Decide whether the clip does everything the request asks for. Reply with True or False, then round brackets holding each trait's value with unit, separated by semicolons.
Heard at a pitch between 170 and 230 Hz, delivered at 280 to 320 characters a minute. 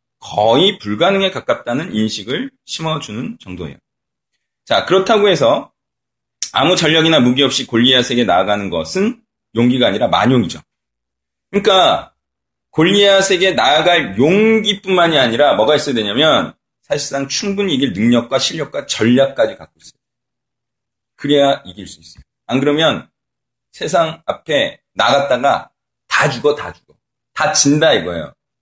False (135 Hz; 305 characters per minute)